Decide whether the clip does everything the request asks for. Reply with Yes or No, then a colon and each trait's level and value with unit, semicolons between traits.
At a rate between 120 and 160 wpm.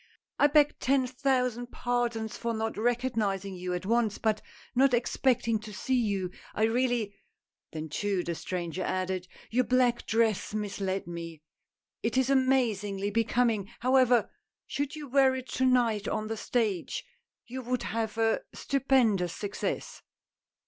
Yes: average, 150 wpm